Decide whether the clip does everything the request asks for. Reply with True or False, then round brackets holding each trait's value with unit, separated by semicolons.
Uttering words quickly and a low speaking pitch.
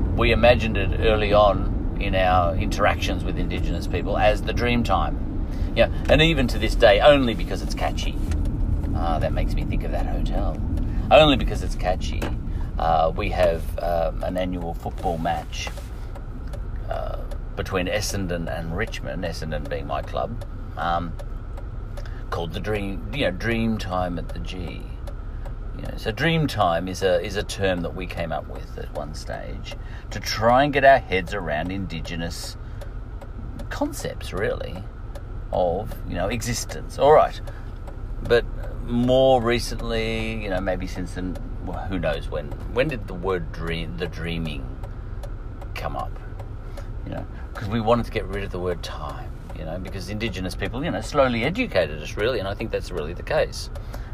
False (165 wpm; 95 Hz)